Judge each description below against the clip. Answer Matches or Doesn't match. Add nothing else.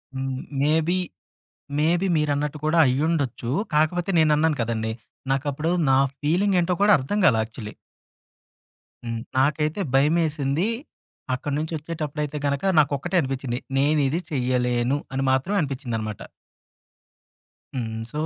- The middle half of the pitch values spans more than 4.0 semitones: Doesn't match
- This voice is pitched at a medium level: Matches